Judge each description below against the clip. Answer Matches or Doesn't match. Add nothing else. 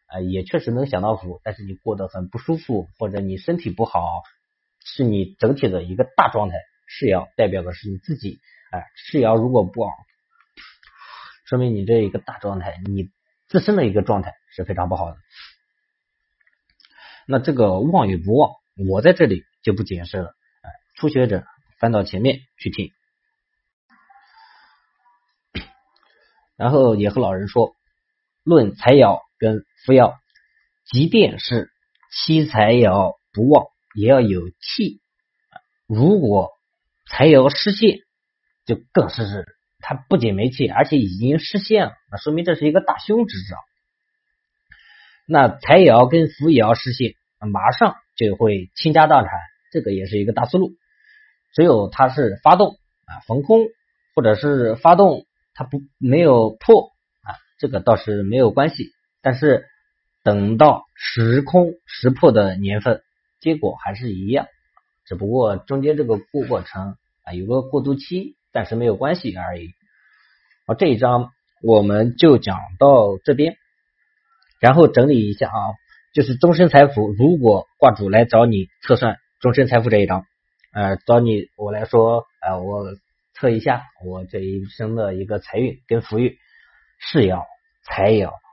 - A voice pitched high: Doesn't match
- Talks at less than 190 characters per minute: Doesn't match